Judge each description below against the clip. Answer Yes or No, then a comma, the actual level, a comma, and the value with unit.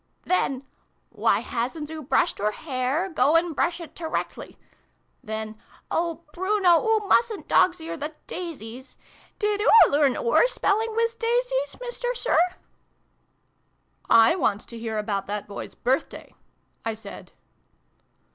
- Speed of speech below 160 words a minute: Yes, average, 150 wpm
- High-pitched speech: Yes, very high, 325 Hz